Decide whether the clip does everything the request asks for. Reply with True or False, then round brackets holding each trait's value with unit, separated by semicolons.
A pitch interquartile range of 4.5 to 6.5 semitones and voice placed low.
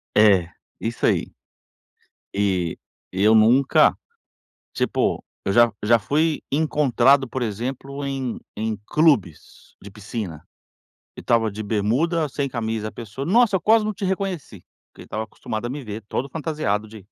True (5.3 semitones; 120 Hz)